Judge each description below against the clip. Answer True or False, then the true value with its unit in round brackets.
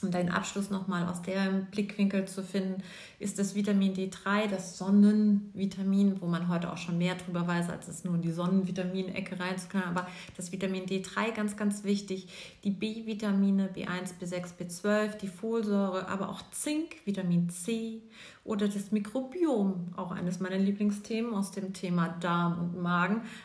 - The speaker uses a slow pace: False (160 wpm)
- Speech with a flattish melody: True (2.1 semitones)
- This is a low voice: False (195 Hz)